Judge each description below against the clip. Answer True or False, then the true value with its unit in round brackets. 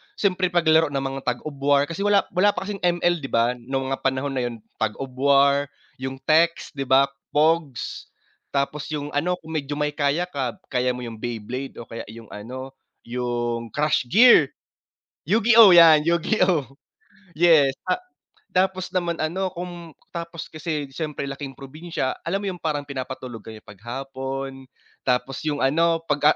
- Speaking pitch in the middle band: True (145 Hz)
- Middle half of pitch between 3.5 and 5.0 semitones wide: True (4.2 semitones)